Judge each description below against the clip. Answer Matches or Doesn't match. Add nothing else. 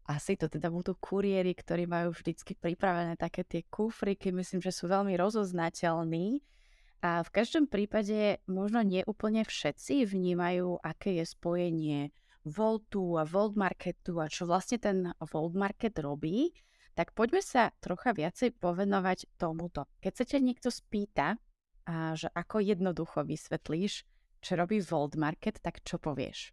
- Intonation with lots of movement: Doesn't match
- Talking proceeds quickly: Doesn't match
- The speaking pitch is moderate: Matches